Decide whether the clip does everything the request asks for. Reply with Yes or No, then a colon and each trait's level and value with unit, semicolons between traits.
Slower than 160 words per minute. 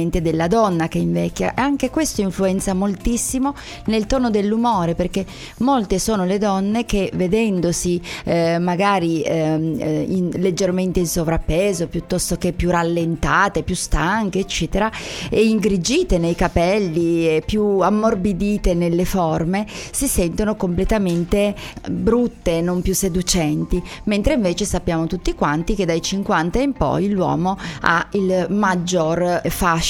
Yes: average, 125 wpm